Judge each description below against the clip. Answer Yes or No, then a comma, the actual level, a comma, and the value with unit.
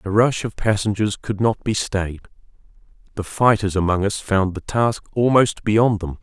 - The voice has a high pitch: No, low, 105 Hz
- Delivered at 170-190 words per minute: Yes, average, 175 wpm